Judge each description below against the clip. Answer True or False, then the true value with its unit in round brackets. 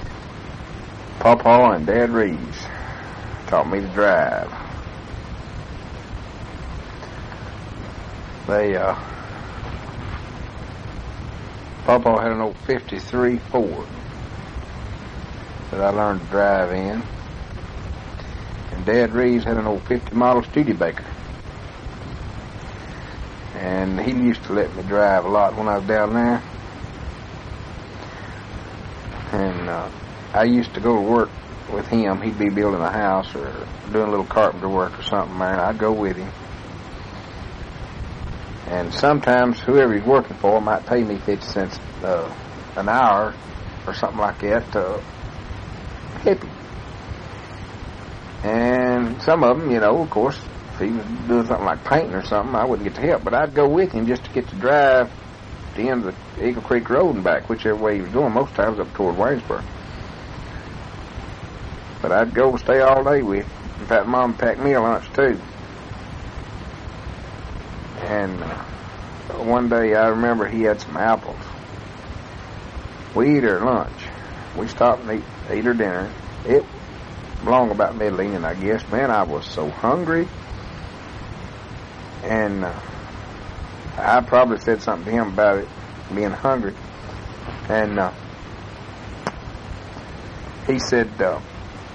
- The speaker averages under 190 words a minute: True (140 wpm)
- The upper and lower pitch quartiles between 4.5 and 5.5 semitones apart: False (3.2 semitones)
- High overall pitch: False (105 Hz)